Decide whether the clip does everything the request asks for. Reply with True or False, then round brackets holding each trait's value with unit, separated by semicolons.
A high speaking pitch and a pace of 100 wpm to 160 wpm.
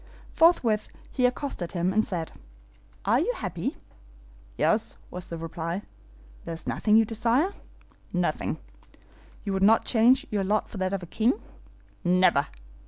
True (205 Hz; 145 wpm)